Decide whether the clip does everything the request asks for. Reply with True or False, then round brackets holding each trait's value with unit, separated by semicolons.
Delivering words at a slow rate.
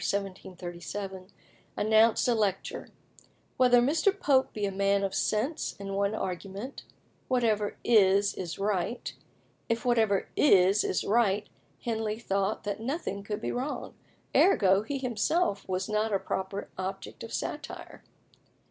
True (130 wpm)